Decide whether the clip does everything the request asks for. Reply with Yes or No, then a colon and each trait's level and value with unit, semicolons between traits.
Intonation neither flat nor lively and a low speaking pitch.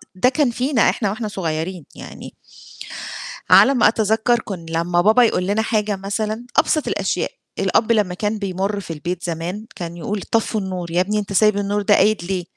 No: average, 3.4 semitones; high, 205 Hz